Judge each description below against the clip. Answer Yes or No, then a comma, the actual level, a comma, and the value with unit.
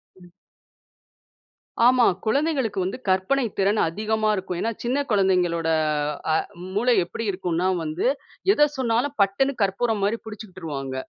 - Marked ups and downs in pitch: No, average, 4.8 semitones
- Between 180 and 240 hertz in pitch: Yes, high, 205 Hz